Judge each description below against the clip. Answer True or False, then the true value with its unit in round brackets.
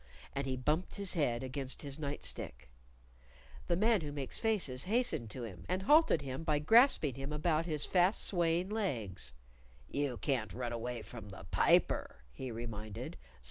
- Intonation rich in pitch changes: True (6.7 semitones)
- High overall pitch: False (140 Hz)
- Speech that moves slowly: False (165 wpm)